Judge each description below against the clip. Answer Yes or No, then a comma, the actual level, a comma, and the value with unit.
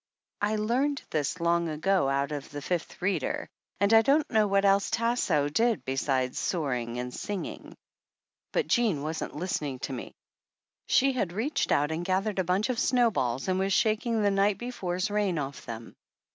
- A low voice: No, high, 190 Hz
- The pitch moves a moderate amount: No, wide, 6.7 semitones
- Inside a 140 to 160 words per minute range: No, average, 170 wpm